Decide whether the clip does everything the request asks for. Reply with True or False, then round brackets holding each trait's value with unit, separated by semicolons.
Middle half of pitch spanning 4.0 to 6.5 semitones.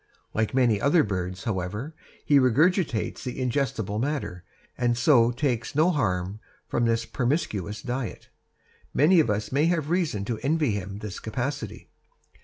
True (5.5 semitones)